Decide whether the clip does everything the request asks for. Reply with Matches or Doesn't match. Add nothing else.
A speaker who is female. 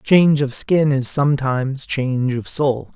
Doesn't match